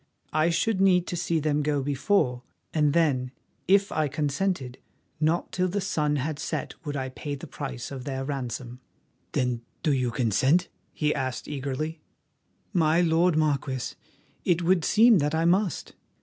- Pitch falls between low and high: Yes, medium, 150 Hz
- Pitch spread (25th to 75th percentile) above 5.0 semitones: No, average, 4.3 semitones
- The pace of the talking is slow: No, average, 160 wpm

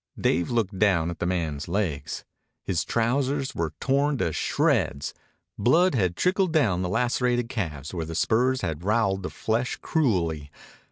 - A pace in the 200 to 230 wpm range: No, average, 150 wpm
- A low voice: Yes, low, 100 Hz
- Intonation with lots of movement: Yes, wide, 6.8 semitones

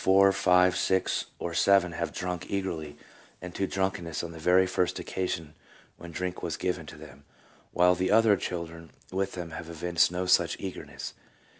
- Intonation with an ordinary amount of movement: No, narrow, 2.1 semitones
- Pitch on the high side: No, very low, 90 Hz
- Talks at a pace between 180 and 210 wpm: No, average, 170 wpm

